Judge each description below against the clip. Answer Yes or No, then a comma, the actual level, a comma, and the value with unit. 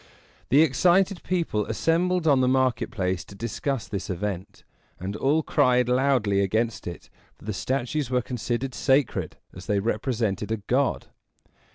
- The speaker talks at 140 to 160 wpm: Yes, average, 150 wpm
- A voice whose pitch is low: Yes, low, 125 Hz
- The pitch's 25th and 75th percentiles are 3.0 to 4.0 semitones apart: No, average, 5.0 semitones